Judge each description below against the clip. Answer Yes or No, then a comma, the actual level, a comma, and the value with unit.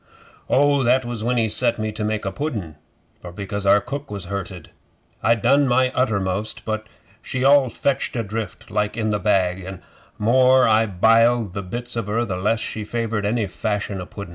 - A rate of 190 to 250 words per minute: Yes, average, 195 wpm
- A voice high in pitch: No, low, 110 Hz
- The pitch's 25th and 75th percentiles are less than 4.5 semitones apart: Yes, average, 3.3 semitones